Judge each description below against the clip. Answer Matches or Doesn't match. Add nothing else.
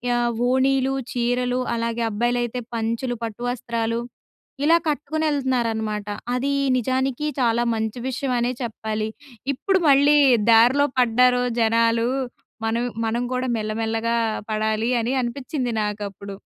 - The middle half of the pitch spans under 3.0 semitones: Matches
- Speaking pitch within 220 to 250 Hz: Matches